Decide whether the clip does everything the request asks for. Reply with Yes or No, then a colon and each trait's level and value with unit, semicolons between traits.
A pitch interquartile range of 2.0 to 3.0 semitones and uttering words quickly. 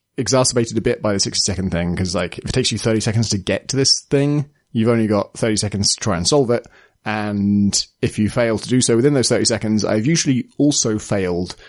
No: average, 3.5 semitones; fast, 235 wpm